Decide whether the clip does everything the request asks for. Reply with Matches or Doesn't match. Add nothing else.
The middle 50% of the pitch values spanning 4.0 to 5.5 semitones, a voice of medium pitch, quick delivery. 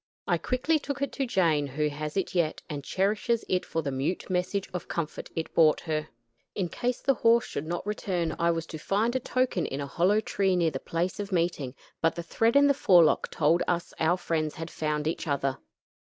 Matches